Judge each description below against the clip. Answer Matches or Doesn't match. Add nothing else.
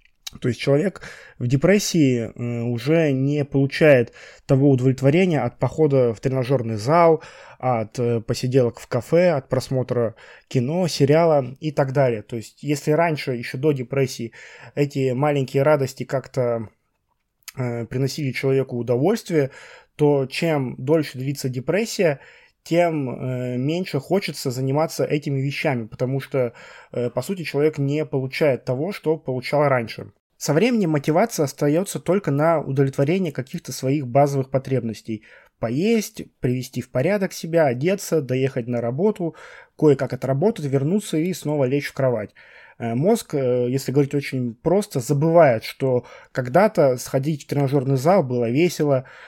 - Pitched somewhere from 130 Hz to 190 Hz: Matches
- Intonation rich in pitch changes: Doesn't match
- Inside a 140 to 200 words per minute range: Doesn't match